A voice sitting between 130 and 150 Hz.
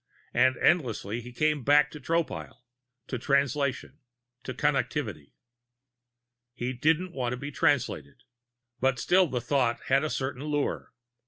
Yes: low, 135 Hz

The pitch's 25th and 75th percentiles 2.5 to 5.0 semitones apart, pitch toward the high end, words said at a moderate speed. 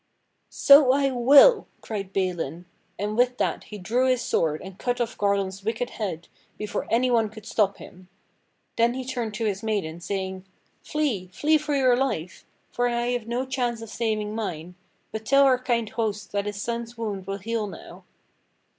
Yes: average, 3.9 semitones; high, 225 Hz; average, 180 wpm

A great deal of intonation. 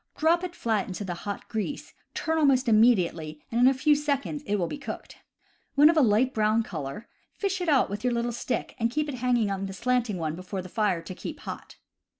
Yes: wide, 6.1 semitones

